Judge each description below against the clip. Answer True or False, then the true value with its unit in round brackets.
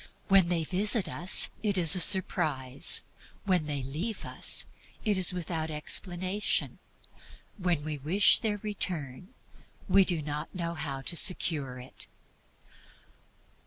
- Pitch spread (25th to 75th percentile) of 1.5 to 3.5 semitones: False (4.1 semitones)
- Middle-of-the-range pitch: True (175 Hz)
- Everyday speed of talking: False (125 wpm)